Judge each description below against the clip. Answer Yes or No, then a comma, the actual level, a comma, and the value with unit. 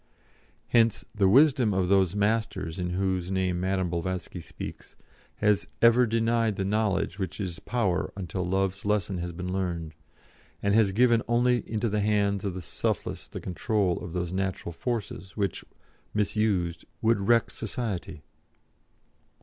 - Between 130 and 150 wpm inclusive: Yes, average, 145 wpm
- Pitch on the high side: No, low, 100 Hz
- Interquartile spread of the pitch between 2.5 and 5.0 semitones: Yes, average, 3.2 semitones